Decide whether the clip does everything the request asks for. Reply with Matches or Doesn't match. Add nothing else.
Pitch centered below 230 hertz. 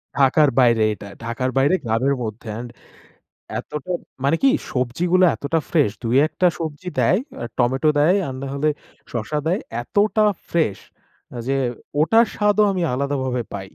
Matches